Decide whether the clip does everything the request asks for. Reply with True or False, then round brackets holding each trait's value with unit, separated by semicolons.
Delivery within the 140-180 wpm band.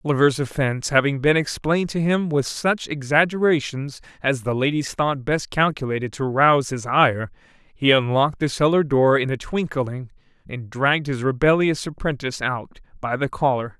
True (160 wpm)